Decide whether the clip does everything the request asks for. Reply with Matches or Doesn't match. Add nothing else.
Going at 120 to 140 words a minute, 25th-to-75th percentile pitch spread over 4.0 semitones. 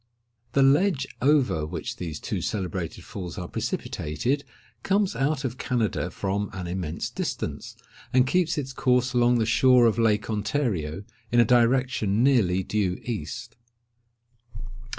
Matches